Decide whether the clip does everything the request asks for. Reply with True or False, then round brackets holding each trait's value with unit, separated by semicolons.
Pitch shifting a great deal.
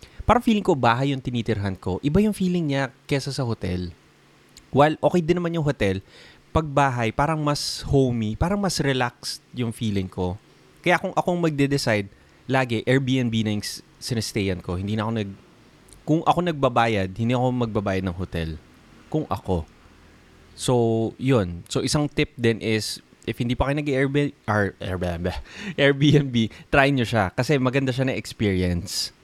True (6.1 semitones)